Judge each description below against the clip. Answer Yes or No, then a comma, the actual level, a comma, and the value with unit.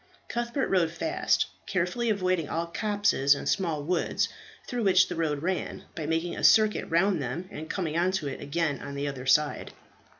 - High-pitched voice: No, medium, 170 Hz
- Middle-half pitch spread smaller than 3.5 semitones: No, average, 4.2 semitones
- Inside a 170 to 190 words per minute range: Yes, average, 180 wpm